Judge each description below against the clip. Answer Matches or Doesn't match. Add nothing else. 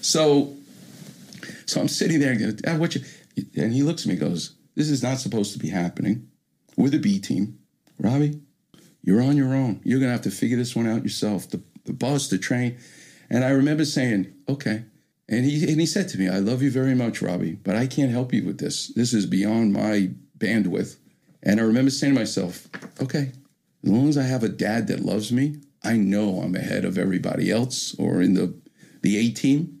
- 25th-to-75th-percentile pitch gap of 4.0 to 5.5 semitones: Matches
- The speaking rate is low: Doesn't match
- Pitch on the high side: Doesn't match